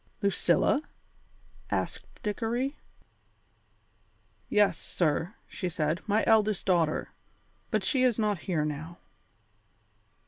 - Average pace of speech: No, slow, 95 wpm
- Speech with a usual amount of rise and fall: Yes, average, 4.9 semitones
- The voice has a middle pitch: No, high, 200 Hz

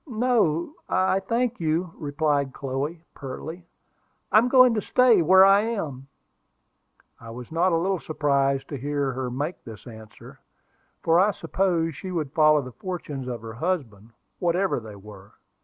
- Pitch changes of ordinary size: No, wide, 5.9 semitones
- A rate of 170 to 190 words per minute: No, average, 155 wpm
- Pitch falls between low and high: Yes, medium, 160 Hz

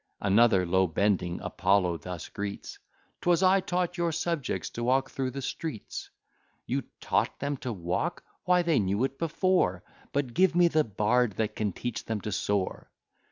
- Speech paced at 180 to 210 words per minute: No, average, 165 wpm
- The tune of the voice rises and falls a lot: Yes, wide, 8.8 semitones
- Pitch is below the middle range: Yes, low, 120 Hz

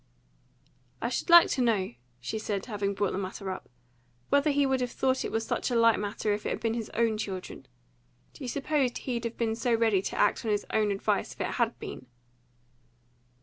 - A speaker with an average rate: No, fast, 215 wpm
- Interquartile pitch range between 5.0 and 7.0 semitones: No, average, 3.3 semitones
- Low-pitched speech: No, high, 225 Hz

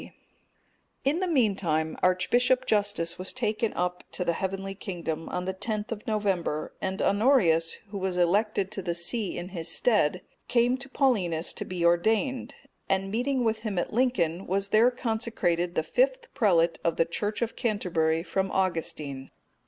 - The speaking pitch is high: Yes, high, 195 Hz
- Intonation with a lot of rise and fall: No, average, 4.9 semitones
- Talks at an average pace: Yes, average, 160 wpm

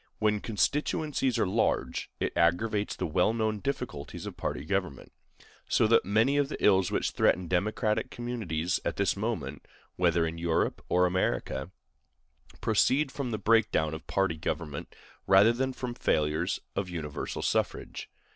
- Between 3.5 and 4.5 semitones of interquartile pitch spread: No, wide, 5.4 semitones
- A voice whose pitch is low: Yes, low, 100 Hz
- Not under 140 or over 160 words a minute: Yes, average, 150 wpm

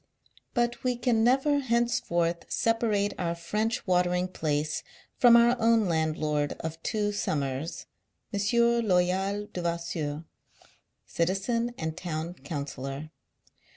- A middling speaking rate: No, slow, 105 wpm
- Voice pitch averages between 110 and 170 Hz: No, medium, 180 Hz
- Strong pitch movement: Yes, wide, 6.1 semitones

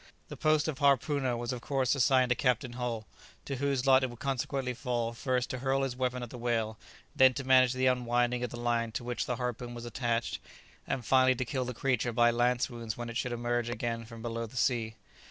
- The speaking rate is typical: No, fast, 225 wpm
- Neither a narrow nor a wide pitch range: No, narrow, 1.6 semitones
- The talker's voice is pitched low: Yes, low, 125 Hz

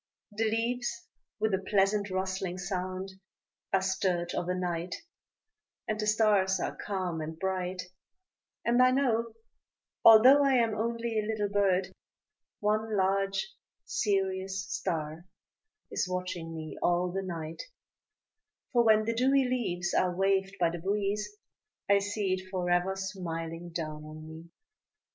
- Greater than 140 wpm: No, slow, 135 wpm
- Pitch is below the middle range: No, high, 190 Hz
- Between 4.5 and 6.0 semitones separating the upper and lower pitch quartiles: No, average, 3.3 semitones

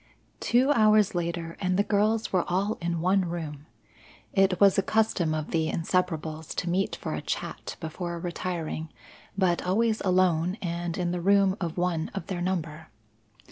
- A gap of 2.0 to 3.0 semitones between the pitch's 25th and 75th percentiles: Yes, average, 2.7 semitones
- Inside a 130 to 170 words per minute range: Yes, average, 165 wpm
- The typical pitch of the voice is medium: Yes, medium, 180 Hz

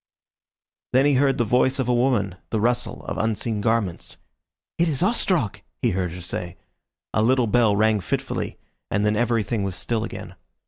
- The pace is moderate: Yes, average, 175 wpm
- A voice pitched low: Yes, low, 115 Hz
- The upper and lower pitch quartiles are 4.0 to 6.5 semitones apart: No, average, 3.5 semitones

